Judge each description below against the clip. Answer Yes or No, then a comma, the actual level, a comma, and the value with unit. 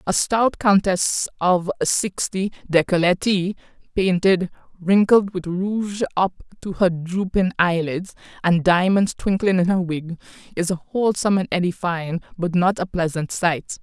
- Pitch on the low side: No, medium, 185 Hz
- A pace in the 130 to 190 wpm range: Yes, slow, 135 wpm